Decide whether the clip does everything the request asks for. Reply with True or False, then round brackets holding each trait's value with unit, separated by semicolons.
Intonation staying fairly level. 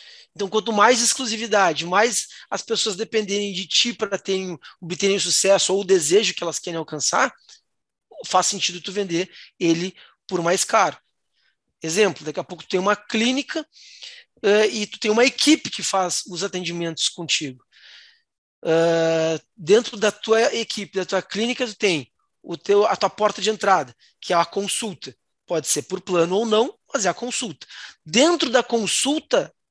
False (4.2 semitones)